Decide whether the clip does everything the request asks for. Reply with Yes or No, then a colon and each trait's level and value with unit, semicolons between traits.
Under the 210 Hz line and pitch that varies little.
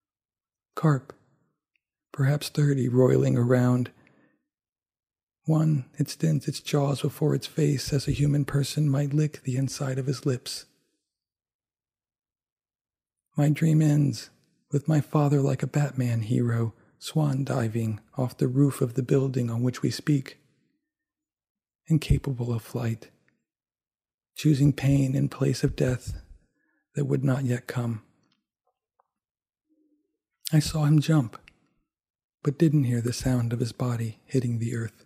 No: medium, 140 Hz; average, 3.1 semitones